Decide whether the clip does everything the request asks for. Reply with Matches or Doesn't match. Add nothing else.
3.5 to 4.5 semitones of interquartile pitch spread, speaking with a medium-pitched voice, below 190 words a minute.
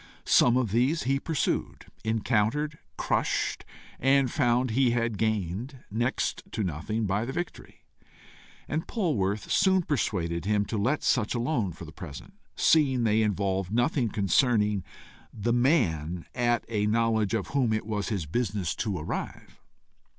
Doesn't match